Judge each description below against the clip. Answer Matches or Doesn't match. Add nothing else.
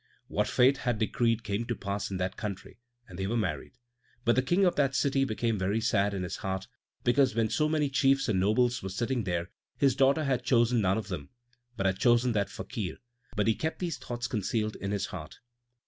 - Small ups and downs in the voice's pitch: Doesn't match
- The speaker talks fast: Matches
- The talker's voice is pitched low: Matches